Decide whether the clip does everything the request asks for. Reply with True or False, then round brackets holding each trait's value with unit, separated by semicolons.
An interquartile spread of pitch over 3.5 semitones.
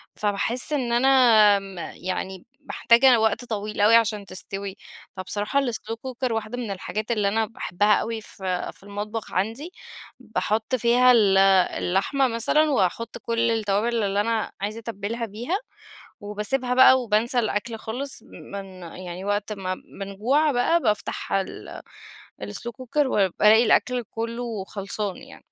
False (3.1 semitones)